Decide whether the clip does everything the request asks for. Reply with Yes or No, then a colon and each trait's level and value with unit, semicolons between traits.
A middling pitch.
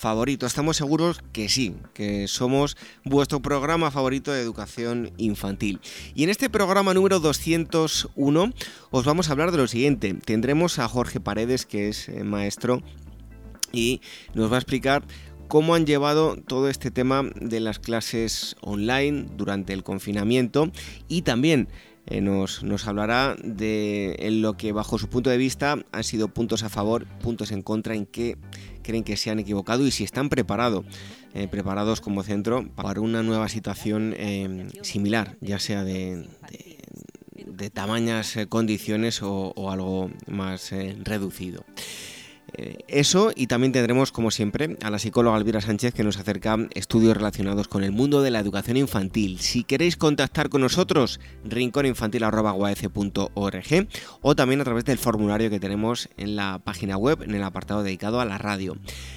No: low, 110 Hz